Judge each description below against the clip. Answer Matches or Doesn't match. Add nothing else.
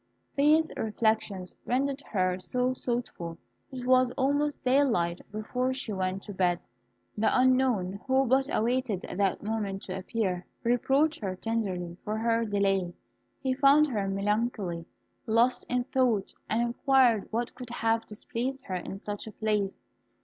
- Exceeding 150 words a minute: Doesn't match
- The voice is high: Matches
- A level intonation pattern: Doesn't match